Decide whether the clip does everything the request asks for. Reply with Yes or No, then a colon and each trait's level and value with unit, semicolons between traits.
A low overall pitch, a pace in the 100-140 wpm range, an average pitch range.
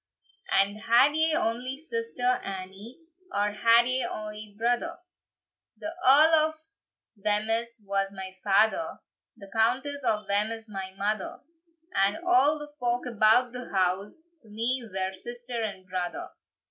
No: high, 225 Hz; slow, 135 wpm; average, 4.1 semitones